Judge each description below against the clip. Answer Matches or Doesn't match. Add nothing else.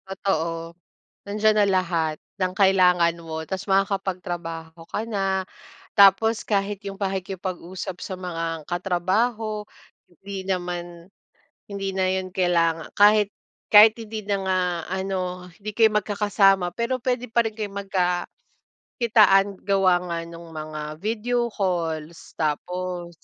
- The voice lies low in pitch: Doesn't match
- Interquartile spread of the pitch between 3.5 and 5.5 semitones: Doesn't match